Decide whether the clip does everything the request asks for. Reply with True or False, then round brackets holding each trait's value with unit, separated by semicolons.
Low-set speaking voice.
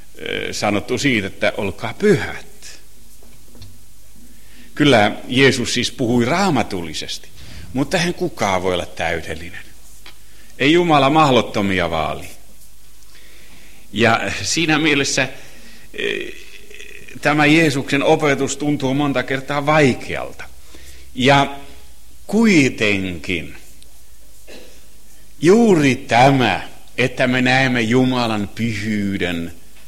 True (125 Hz)